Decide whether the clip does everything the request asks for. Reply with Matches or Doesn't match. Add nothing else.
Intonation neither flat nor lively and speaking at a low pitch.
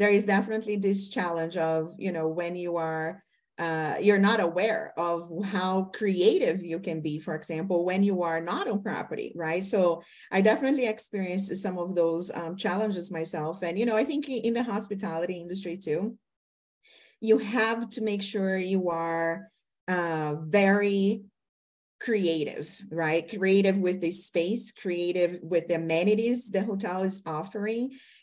Doesn't match